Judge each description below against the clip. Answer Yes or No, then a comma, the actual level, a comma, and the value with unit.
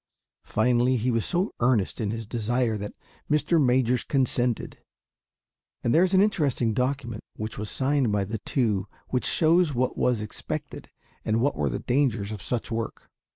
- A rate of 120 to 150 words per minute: No, average, 165 wpm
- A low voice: Yes, low, 120 Hz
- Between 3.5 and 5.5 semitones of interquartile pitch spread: Yes, average, 3.8 semitones